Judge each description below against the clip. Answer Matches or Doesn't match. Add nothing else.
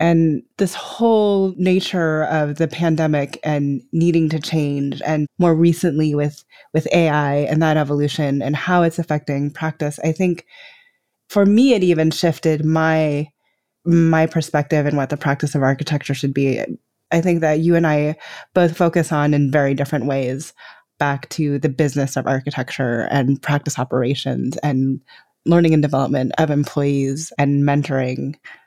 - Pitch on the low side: Doesn't match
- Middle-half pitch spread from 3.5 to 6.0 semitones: Doesn't match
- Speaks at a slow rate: Doesn't match